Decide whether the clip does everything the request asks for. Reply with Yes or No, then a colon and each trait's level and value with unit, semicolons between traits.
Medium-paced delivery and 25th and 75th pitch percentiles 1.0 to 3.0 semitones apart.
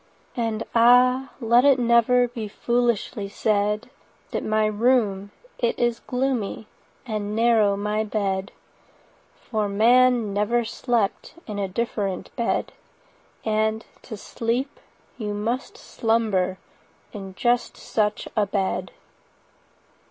No: slow, 115 wpm; narrow, 2.6 semitones